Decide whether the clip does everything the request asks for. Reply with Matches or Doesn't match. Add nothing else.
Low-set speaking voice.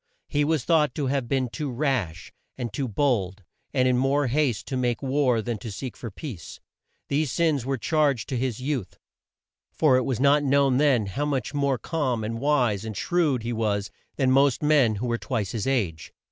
Matches